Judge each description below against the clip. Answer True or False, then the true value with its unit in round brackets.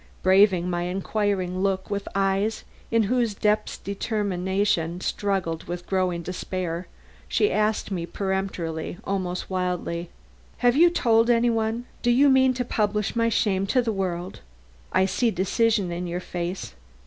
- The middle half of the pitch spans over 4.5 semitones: False (3.5 semitones)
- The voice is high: True (195 Hz)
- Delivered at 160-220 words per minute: False (145 wpm)